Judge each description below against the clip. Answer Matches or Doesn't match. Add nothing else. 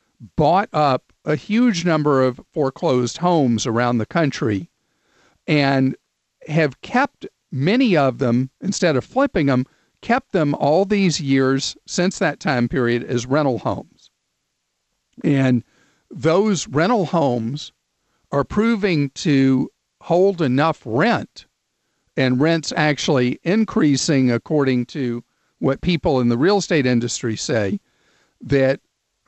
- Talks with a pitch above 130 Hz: Matches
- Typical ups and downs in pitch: Doesn't match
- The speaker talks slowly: Matches